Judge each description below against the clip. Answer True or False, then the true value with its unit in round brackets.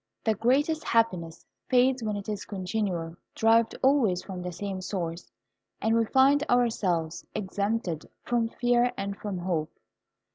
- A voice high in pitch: True (210 Hz)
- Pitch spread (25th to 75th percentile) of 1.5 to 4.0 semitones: False (4.8 semitones)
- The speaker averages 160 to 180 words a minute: False (140 wpm)